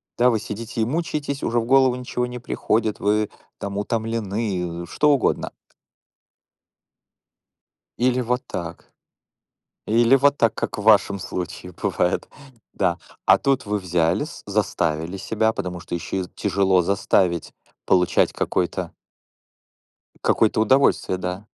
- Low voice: Yes, low, 105 Hz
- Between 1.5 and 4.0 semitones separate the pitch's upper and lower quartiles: No, average, 5.0 semitones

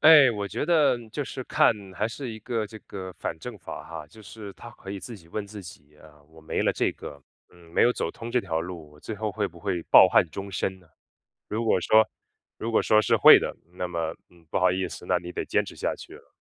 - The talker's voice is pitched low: Yes, very low, 95 Hz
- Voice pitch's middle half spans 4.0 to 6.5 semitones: Yes, average, 4.6 semitones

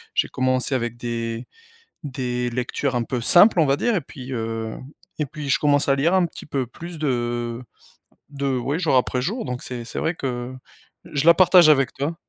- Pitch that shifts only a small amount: No, average, 3.8 semitones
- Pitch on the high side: No, low, 135 Hz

